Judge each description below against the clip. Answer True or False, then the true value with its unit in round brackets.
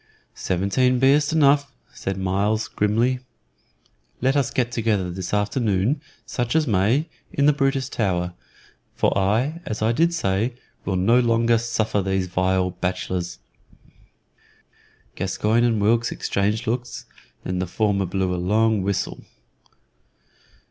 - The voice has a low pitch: True (110 Hz)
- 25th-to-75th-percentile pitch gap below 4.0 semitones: False (4.5 semitones)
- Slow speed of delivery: True (130 wpm)